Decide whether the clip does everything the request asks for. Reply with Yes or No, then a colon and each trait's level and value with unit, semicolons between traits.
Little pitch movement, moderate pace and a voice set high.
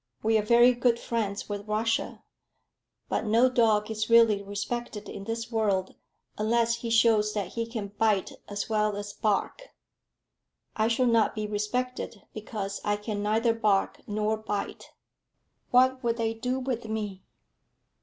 Yes: narrow, 1.9 semitones; average, 150 wpm; high, 220 Hz